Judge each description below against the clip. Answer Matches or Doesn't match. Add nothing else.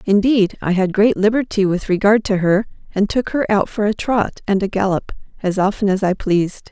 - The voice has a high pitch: Matches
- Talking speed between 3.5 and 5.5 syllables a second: Matches